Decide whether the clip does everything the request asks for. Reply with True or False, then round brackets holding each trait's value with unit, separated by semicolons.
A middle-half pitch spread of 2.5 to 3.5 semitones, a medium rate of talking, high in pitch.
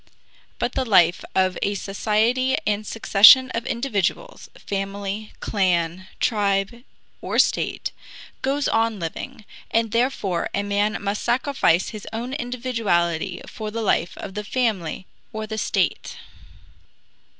False (3.2 semitones; 125 wpm; 210 Hz)